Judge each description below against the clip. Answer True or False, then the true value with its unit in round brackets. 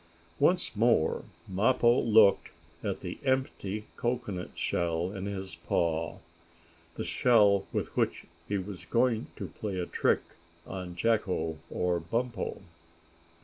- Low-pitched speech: True (100 Hz)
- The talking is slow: True (120 wpm)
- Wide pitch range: False (4.5 semitones)